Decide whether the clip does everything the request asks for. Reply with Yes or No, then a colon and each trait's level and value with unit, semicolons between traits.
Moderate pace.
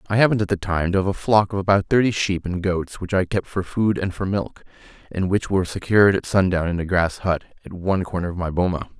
No: fast, 260 wpm